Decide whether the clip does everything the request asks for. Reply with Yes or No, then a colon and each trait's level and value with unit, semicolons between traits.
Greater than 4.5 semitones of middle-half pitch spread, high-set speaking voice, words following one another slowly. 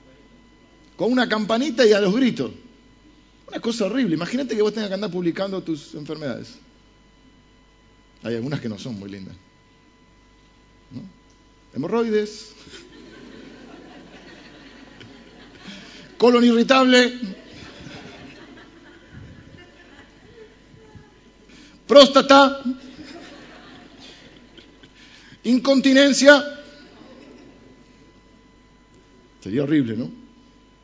Yes: average, 5.3 semitones; high, 240 Hz; slow, 70 wpm